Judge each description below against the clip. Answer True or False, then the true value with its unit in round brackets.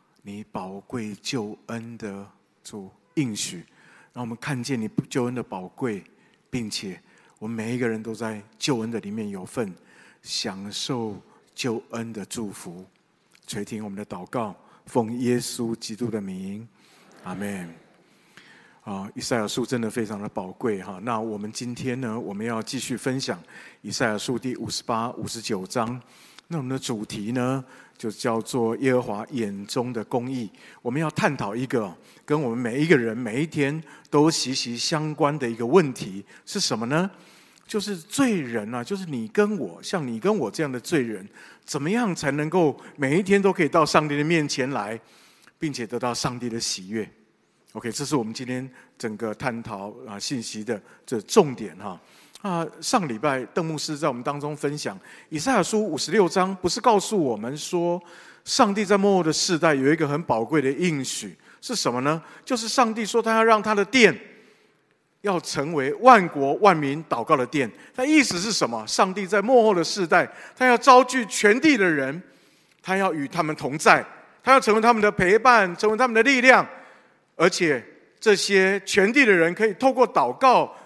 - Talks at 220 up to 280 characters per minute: True (255 characters per minute)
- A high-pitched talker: False (140 Hz)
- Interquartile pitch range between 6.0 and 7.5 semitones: False (8.8 semitones)